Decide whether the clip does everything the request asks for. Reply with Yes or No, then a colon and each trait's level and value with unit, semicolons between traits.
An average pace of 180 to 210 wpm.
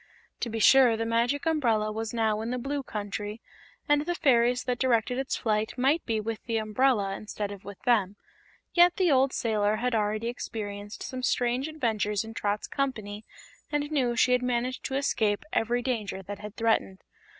Yes: average, 185 wpm